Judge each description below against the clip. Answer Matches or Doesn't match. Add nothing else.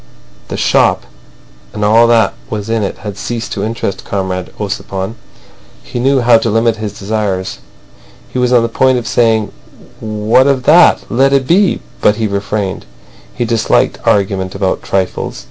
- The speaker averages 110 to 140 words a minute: Doesn't match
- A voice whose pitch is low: Matches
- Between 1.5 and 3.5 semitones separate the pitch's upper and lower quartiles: Matches